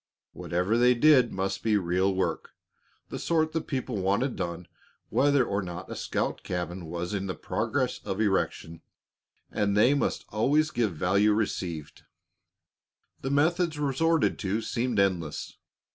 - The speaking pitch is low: Yes, low, 105 Hz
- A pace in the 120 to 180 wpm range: Yes, average, 140 wpm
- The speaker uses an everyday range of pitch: No, wide, 6.4 semitones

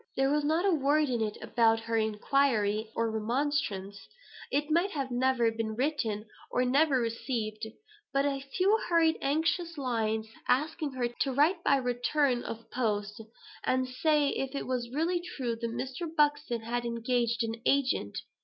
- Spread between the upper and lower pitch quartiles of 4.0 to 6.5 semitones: Yes, average, 4.3 semitones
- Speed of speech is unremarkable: Yes, average, 160 wpm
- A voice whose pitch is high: Yes, very high, 255 Hz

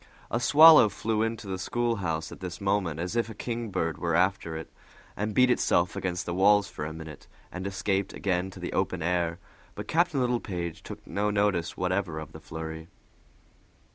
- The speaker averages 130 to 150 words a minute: No, average, 180 wpm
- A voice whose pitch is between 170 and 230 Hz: No, very low, 95 Hz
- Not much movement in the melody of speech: No, average, 4.0 semitones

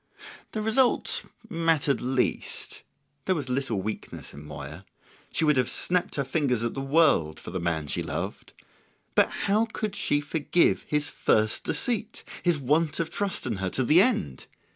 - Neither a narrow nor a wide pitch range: No, wide, 7.8 semitones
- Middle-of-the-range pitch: Yes, medium, 145 Hz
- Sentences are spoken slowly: No, average, 165 wpm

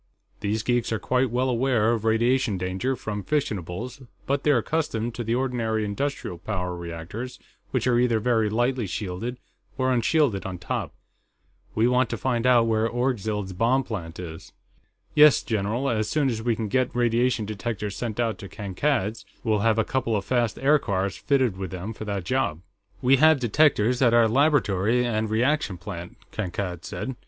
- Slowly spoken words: No, average, 170 wpm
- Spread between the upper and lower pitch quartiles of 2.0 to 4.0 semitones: Yes, average, 3.7 semitones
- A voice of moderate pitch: No, low, 115 Hz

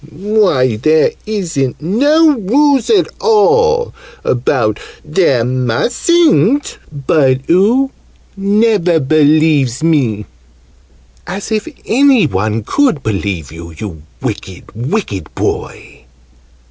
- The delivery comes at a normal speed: No, slow, 95 wpm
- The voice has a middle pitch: Yes, medium, 160 Hz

